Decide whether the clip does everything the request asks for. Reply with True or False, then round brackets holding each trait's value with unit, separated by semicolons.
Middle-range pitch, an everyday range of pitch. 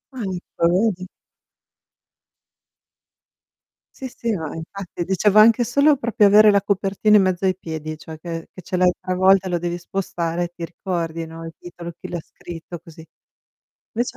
True (180 Hz; 3.2 semitones)